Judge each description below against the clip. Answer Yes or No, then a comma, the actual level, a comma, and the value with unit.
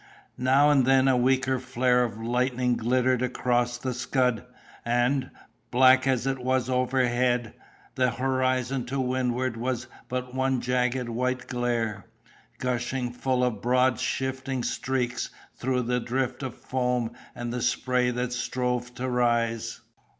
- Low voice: Yes, low, 125 Hz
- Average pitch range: No, narrow, 1.0 semitones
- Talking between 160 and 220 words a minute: No, slow, 135 wpm